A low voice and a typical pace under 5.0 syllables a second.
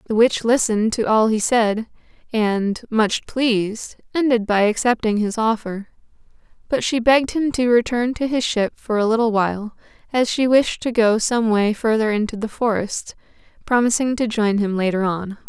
No: high, 225 Hz; 4.8 syllables/s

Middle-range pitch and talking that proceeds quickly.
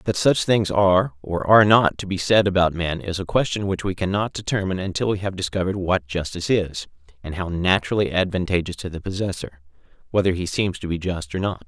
No: very low, 95 Hz; fast, 210 wpm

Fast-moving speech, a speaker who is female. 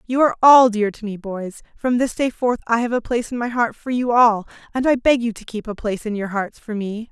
Yes: fast, 285 wpm; female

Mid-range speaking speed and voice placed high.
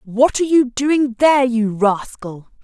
Yes: average, 160 wpm; high, 245 Hz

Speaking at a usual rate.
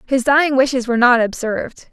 Yes: average, 190 wpm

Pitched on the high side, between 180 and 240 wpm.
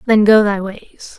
Yes: high, 210 Hz; fast, 205 wpm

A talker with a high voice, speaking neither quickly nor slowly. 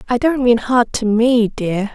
No: high, 235 Hz; fast, 215 wpm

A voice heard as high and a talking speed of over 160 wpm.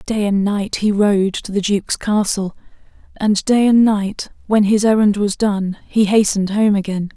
Yes: high, 205 Hz; average, 185 wpm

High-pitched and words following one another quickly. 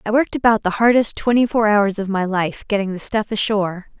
Yes: high, 210 Hz; fast, 225 wpm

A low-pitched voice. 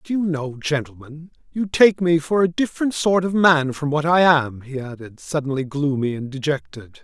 No: medium, 150 Hz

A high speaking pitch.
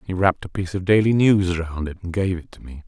No: very low, 90 Hz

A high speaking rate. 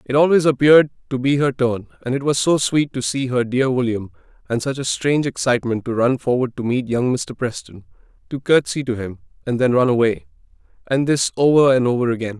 Yes: fast, 215 wpm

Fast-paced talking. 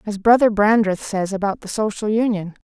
No: average, 180 wpm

